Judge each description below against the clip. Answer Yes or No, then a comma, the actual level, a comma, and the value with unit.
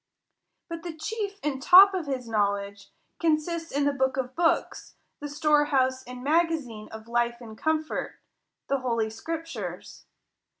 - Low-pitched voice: No, very high, 280 Hz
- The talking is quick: No, average, 140 wpm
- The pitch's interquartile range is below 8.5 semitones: Yes, wide, 5.4 semitones